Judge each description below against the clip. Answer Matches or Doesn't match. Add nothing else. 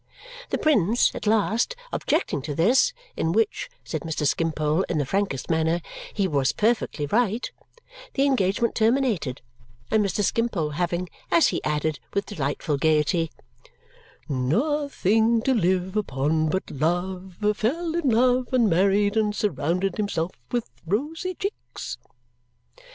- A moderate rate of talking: Doesn't match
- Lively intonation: Matches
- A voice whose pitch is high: Matches